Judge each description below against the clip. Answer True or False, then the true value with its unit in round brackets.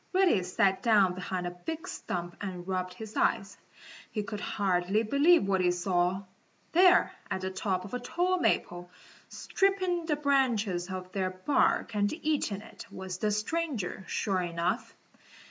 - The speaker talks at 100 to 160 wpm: True (155 wpm)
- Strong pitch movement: True (7.3 semitones)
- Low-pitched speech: False (200 Hz)